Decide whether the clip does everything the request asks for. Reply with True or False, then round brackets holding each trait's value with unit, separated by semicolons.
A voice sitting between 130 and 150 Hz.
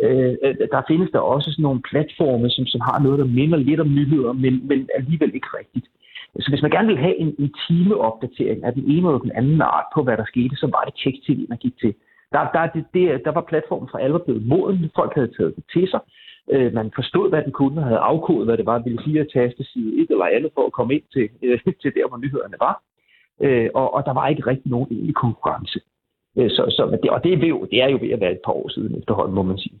True (140 Hz)